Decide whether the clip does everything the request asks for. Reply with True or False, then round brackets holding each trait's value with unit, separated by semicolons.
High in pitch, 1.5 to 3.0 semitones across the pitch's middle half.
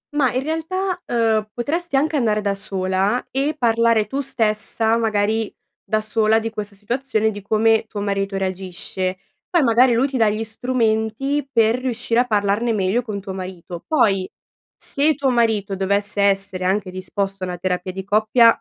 False (220 Hz; 3.6 semitones)